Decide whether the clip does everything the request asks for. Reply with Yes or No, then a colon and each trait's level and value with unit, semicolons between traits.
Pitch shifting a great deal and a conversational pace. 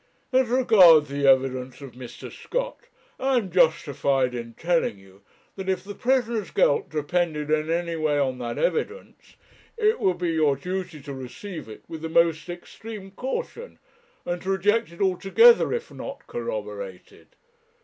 Yes: wide, 7.3 semitones; average, 155 wpm